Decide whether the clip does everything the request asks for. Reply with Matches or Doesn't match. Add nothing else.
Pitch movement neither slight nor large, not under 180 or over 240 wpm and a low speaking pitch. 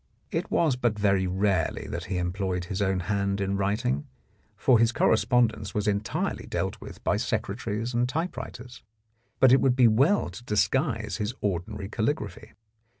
Doesn't match